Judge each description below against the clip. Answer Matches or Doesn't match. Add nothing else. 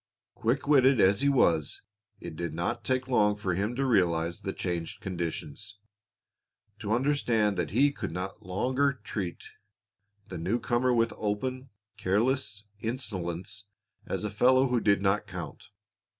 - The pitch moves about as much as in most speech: Doesn't match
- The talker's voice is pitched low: Matches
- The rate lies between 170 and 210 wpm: Doesn't match